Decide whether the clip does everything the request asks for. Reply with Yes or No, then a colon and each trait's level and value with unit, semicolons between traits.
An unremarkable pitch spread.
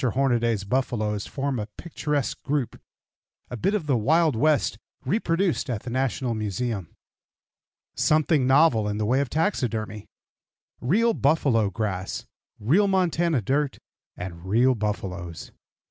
No: wide, 6.0 semitones